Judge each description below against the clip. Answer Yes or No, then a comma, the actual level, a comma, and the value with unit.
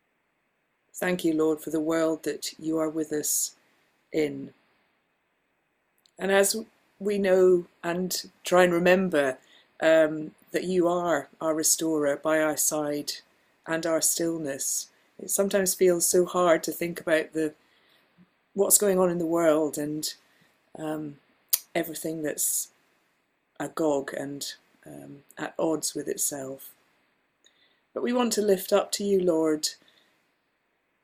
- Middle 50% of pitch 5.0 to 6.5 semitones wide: No, average, 2.9 semitones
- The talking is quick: No, slow, 130 wpm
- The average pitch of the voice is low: No, medium, 160 Hz